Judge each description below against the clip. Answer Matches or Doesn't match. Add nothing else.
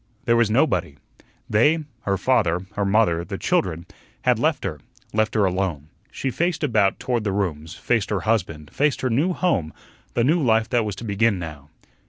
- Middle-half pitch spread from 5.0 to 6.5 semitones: Matches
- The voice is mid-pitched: Doesn't match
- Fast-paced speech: Doesn't match